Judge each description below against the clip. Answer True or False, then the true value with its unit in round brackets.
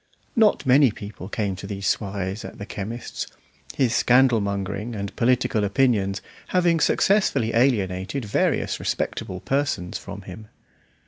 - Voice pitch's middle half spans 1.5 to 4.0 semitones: False (4.5 semitones)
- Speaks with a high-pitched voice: False (105 Hz)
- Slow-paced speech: True (130 wpm)